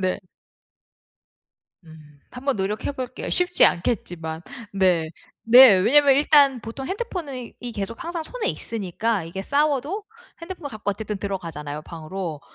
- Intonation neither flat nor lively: No, wide, 7.6 semitones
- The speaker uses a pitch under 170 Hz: No, high, 225 Hz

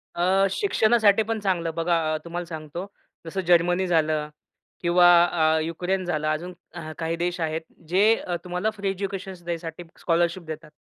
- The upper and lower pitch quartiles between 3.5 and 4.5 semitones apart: No, average, 2.7 semitones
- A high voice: No, medium, 175 Hz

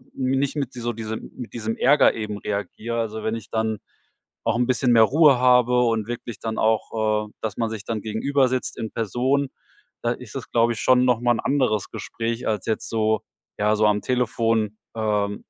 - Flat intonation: Yes, narrow, 2.3 semitones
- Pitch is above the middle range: No, low, 115 Hz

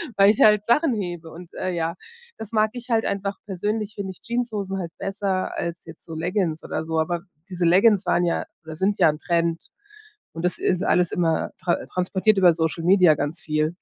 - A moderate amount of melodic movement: Yes, average, 3.4 semitones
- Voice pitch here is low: No, medium, 180 Hz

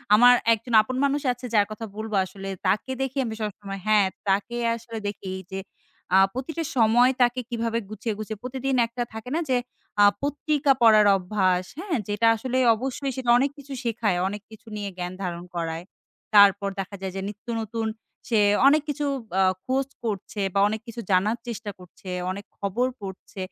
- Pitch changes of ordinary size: Yes, average, 3.9 semitones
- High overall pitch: Yes, high, 220 Hz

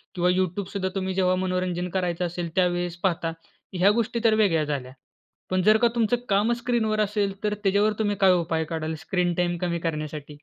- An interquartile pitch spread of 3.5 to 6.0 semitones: No, average, 3.1 semitones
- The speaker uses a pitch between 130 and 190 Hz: Yes, medium, 185 Hz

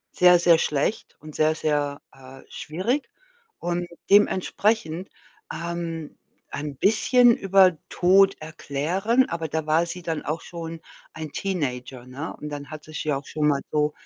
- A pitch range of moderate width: Yes, average, 3.3 semitones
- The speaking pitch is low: No, medium, 160 Hz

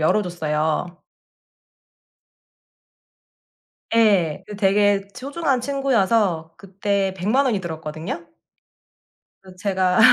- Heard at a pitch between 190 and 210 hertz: Yes, high, 195 Hz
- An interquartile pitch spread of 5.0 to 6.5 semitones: No, average, 4.0 semitones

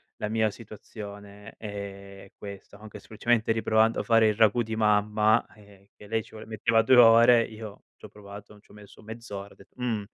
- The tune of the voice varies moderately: No, narrow, 1.7 semitones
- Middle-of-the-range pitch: No, low, 105 Hz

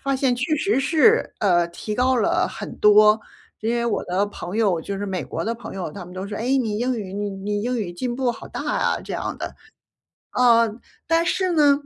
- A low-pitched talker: No, high, 225 Hz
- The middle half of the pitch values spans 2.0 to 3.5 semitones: No, average, 4.3 semitones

